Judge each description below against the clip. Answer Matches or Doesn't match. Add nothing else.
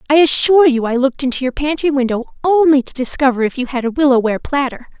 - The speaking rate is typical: Doesn't match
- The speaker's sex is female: Matches